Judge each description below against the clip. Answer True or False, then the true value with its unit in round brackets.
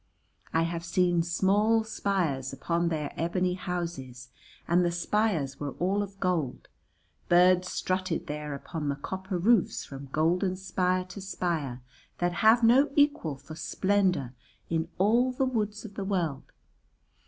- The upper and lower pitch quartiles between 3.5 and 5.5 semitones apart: True (3.8 semitones)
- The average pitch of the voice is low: False (180 Hz)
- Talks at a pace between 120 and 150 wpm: True (140 wpm)